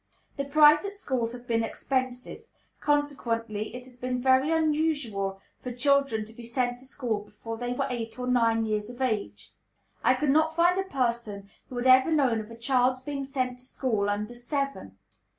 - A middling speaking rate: Yes, average, 185 wpm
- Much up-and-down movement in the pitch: No, average, 3.4 semitones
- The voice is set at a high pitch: Yes, very high, 250 Hz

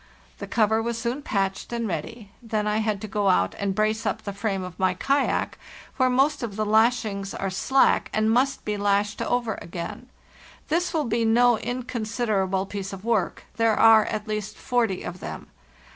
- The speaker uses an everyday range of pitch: Yes, average, 3.0 semitones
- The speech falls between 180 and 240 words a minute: Yes, average, 185 wpm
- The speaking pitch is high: Yes, high, 215 Hz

